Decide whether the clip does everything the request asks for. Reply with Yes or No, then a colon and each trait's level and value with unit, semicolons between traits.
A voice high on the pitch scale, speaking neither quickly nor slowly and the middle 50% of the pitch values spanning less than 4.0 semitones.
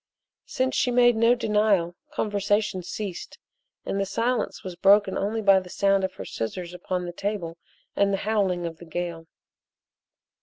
Yes: high, 195 Hz; average, 160 wpm; average, 3.0 semitones